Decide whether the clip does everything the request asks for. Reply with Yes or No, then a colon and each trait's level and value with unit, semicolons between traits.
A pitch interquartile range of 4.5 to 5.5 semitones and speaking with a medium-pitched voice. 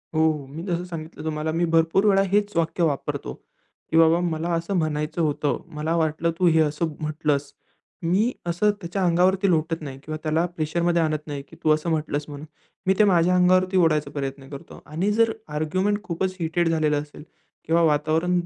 No: narrow, 2.5 semitones; medium, 165 Hz